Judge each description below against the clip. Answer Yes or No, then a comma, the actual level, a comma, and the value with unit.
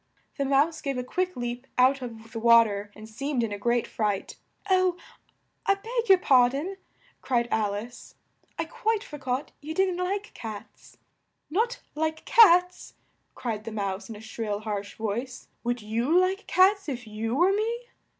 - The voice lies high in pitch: Yes, very high, 255 Hz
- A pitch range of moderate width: No, wide, 8.3 semitones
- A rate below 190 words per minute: Yes, average, 175 wpm